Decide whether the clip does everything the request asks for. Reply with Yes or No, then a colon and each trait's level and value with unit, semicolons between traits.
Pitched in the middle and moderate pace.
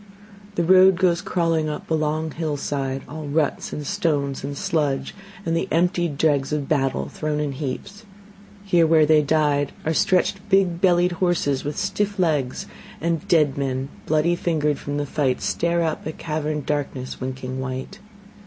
Yes: medium, 155 Hz; average, 160 wpm